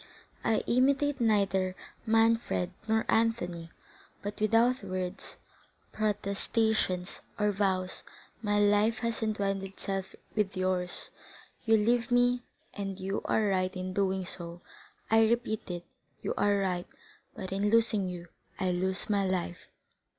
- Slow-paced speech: Yes, slow, 125 wpm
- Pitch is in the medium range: No, high, 200 Hz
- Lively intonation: No, average, 3.1 semitones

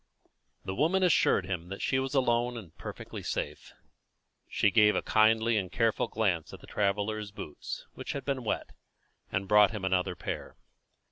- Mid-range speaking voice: No, low, 105 Hz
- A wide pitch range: No, average, 3.6 semitones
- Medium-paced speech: Yes, average, 165 wpm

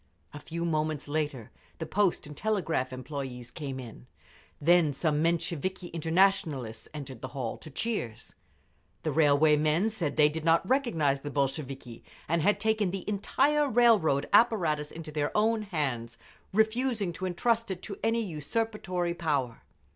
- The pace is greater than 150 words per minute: No, average, 145 wpm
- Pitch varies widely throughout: Yes, wide, 5.8 semitones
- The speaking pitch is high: No, medium, 160 Hz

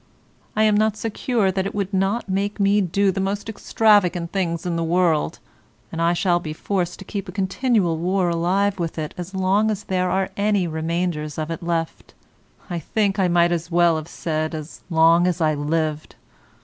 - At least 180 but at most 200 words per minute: Yes, average, 195 wpm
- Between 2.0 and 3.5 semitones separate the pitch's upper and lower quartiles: Yes, average, 3.0 semitones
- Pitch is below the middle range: No, medium, 180 Hz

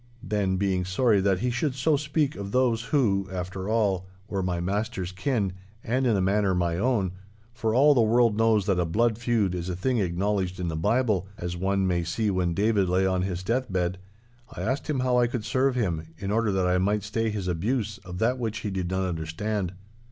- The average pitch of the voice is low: Yes, low, 100 Hz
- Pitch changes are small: No, average, 3.9 semitones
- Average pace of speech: No, fast, 210 wpm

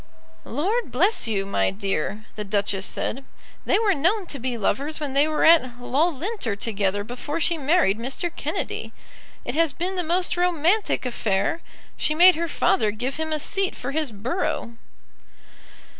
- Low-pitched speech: No, very high, 285 Hz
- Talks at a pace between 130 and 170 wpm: Yes, average, 160 wpm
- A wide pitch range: Yes, wide, 7.2 semitones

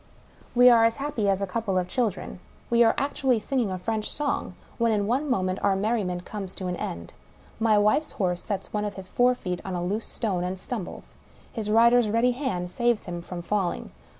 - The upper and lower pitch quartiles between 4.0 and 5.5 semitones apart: Yes, average, 4.3 semitones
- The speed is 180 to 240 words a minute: Yes, fast, 205 wpm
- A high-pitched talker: Yes, high, 210 Hz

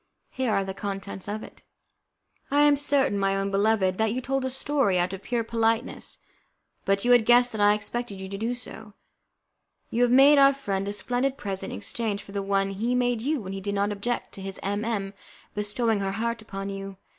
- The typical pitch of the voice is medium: No, high, 210 Hz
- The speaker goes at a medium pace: No, fast, 215 wpm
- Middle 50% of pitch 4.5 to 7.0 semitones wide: No, average, 3.7 semitones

